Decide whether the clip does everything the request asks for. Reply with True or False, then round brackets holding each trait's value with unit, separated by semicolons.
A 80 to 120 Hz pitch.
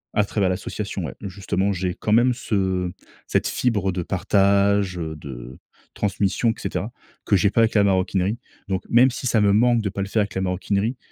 True (100 Hz)